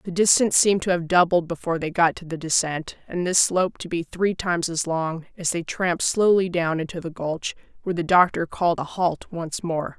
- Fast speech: Yes, fast, 220 wpm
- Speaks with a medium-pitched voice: Yes, medium, 170 Hz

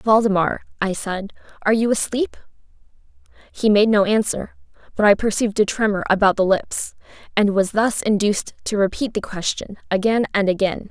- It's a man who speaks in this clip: No, female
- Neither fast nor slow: Yes, average, 160 wpm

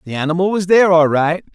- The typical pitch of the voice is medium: Yes, medium, 170 Hz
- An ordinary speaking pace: No, fast, 235 wpm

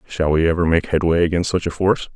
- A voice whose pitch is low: Yes, very low, 85 Hz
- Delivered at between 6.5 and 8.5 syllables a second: Yes, 6.7 syllables/s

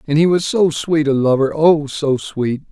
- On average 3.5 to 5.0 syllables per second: Yes, 4.4 syllables/s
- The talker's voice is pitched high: No, medium, 150 Hz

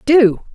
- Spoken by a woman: Yes, female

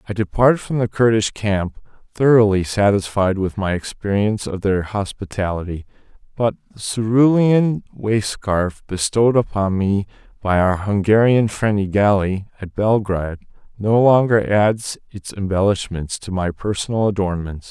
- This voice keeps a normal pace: No, slow, 130 wpm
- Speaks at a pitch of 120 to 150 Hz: No, low, 105 Hz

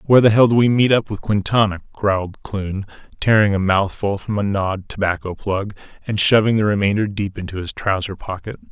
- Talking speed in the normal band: Yes, average, 195 wpm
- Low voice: Yes, low, 100 Hz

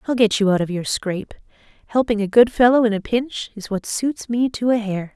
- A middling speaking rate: No, fast, 245 wpm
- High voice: Yes, high, 220 Hz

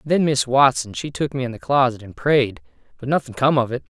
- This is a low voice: Yes, low, 130 Hz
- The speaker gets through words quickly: Yes, fast, 245 wpm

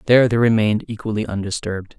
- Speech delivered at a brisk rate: No, average, 150 wpm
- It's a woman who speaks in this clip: No, male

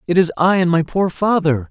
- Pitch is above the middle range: No, medium, 170 Hz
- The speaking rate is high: Yes, fast, 245 wpm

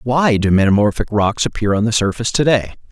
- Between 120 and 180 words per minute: No, fast, 205 wpm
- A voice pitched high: No, low, 110 Hz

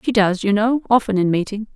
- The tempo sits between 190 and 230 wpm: No, fast, 240 wpm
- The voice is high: Yes, high, 210 Hz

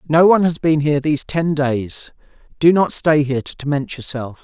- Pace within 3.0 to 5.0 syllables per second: No, 5.6 syllables/s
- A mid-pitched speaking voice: Yes, medium, 150 Hz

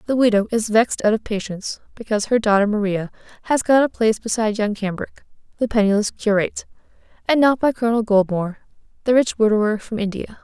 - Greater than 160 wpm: Yes, average, 180 wpm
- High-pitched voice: Yes, high, 215 Hz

